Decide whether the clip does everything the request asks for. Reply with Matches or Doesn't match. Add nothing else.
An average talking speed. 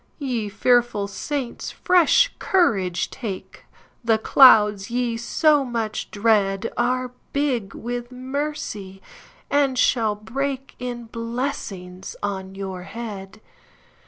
Doesn't match